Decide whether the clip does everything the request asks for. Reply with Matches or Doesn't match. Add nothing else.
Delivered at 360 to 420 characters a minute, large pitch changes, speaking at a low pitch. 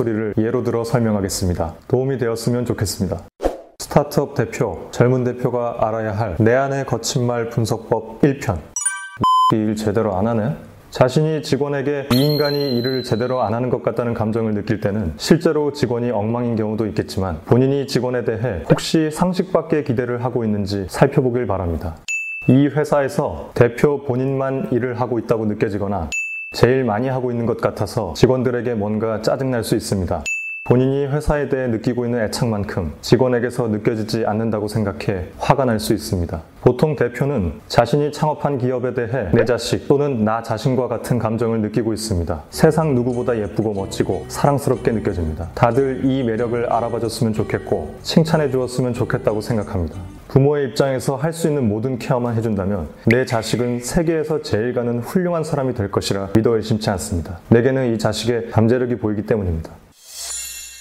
Doesn't match